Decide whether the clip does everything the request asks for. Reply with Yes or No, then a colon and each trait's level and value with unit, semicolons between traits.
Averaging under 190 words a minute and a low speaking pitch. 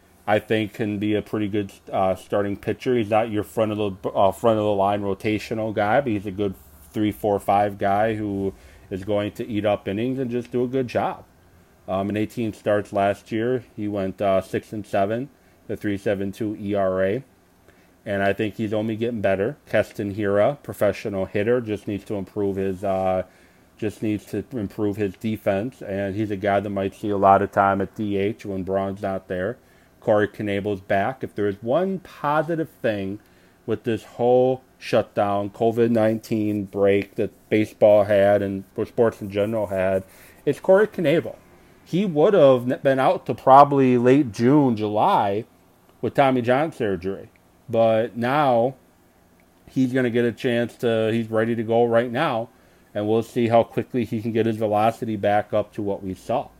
Yes: average, 180 wpm; low, 105 Hz